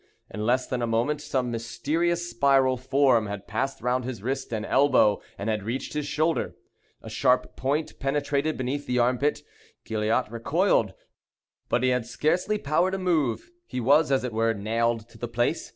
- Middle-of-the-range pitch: No, low, 130 Hz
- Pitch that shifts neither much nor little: Yes, average, 3.9 semitones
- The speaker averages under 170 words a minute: No, average, 175 wpm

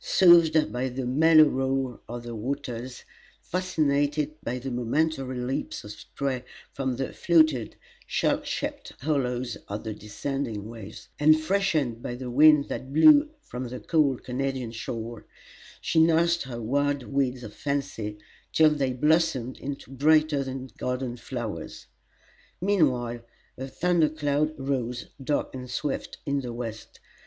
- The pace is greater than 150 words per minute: No, average, 140 wpm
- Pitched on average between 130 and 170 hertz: Yes, low, 135 Hz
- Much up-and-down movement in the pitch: No, average, 3.8 semitones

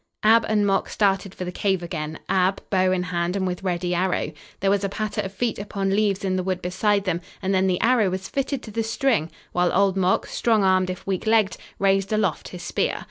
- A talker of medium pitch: No, high, 195 Hz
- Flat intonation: Yes, narrow, 2.0 semitones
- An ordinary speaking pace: No, fast, 230 wpm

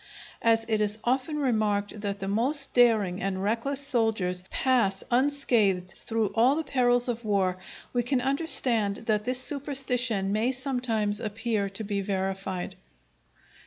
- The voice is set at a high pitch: Yes, high, 225 Hz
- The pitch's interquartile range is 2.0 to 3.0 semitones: No, average, 4.0 semitones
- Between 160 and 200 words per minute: No, average, 140 wpm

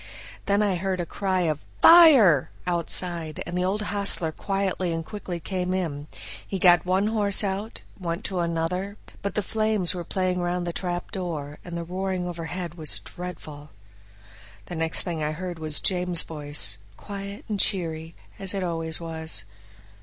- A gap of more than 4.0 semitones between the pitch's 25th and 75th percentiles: No, average, 2.9 semitones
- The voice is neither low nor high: Yes, medium, 180 Hz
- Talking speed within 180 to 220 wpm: No, average, 165 wpm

